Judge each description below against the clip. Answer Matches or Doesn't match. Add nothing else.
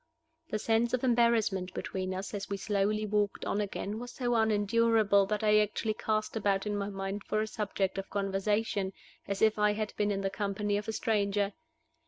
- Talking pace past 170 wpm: Matches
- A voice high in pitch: Matches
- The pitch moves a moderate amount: Doesn't match